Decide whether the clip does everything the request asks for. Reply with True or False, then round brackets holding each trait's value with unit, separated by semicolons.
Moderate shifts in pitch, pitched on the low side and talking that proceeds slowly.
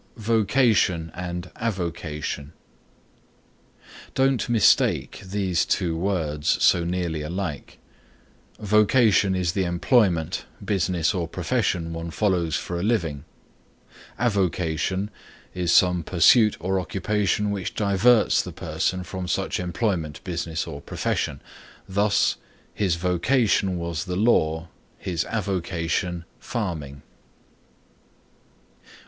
True (3.5 semitones; 90 Hz; 100 wpm)